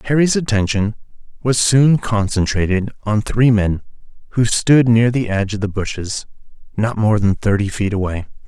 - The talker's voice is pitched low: Yes, low, 110 Hz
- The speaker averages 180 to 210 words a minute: No, average, 155 wpm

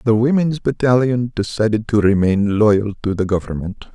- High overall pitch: No, low, 110 Hz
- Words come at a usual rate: Yes, average, 150 wpm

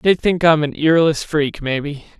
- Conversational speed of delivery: Yes, average, 190 wpm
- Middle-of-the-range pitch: Yes, medium, 155 Hz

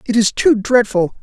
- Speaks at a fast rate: No, average, 195 wpm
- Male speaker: Yes, male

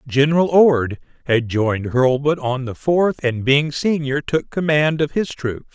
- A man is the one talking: Yes, male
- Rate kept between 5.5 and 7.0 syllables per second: No, 4.2 syllables/s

